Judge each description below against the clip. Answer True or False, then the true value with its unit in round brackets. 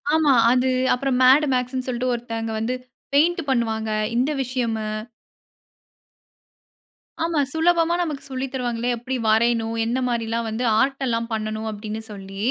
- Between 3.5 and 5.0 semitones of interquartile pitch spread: False (2.9 semitones)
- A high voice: True (245 Hz)